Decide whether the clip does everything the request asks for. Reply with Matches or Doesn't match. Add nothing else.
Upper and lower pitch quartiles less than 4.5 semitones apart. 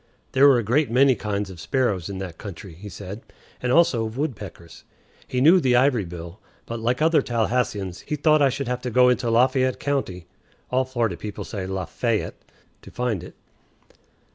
Doesn't match